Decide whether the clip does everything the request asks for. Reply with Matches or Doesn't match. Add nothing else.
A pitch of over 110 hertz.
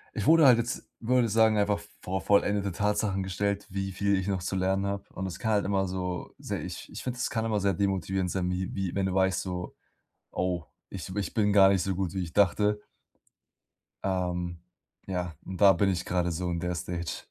Doesn't match